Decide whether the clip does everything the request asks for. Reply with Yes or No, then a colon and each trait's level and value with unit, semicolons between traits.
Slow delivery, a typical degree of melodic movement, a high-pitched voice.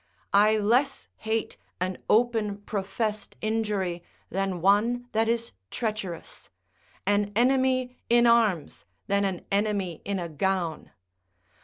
Yes: slow, 115 wpm; average, 3.1 semitones; high, 210 Hz